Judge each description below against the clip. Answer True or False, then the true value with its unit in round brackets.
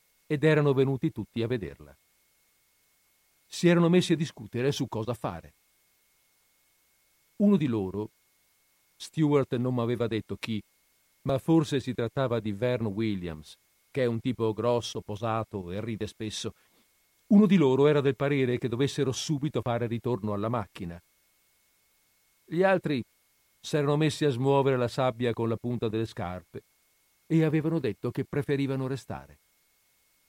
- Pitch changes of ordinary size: True (4.7 semitones)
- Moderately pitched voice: False (125 Hz)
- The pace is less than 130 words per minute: False (145 wpm)